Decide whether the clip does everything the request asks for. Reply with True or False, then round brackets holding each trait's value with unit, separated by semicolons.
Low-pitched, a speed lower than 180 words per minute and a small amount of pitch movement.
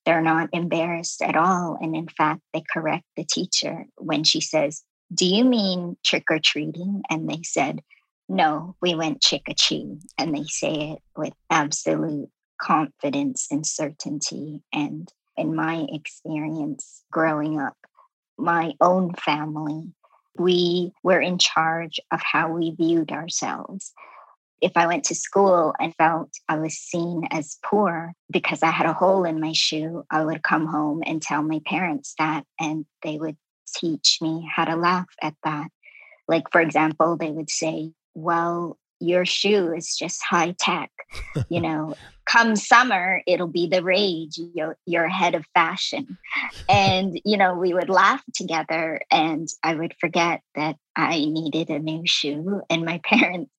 False (165 Hz; 160 wpm; 2.2 semitones)